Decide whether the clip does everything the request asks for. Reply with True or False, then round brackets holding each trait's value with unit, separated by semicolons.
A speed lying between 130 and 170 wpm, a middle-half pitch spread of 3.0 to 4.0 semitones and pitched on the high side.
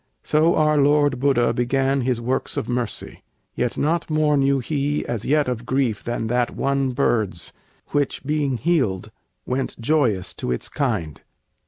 False (155 wpm; 3.4 semitones; 135 Hz)